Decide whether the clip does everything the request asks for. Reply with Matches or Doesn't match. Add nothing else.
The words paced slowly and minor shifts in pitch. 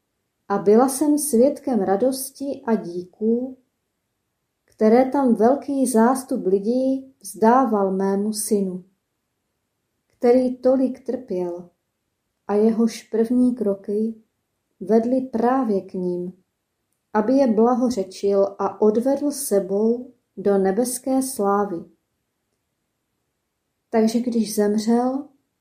Doesn't match